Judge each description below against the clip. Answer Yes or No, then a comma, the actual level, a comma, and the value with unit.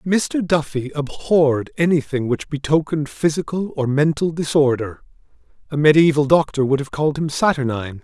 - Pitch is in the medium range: Yes, medium, 150 Hz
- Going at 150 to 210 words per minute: No, slow, 135 wpm